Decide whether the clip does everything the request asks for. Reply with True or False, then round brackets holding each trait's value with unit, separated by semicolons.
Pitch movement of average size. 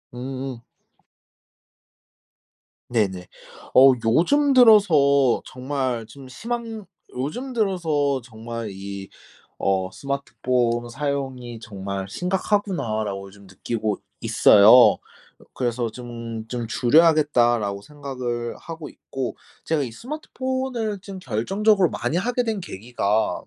False (7.7 semitones)